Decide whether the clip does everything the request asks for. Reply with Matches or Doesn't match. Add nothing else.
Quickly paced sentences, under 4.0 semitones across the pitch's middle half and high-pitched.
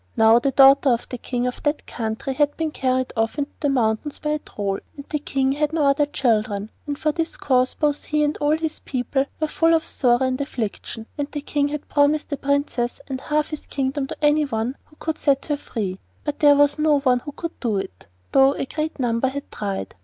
Matches